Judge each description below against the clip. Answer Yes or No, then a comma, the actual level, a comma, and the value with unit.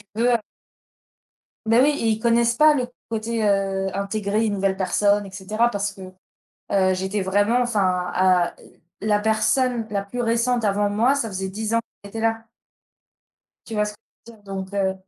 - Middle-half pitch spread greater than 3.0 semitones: No, average, 2.7 semitones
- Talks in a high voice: Yes, high, 210 Hz